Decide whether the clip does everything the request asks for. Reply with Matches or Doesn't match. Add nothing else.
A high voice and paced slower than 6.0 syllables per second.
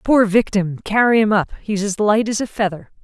Matches